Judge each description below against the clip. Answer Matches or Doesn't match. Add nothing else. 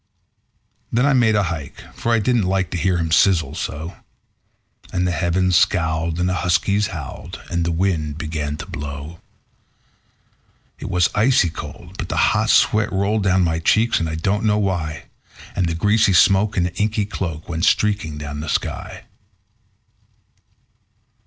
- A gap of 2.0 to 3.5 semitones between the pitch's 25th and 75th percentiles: Doesn't match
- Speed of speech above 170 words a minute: Doesn't match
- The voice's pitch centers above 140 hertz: Doesn't match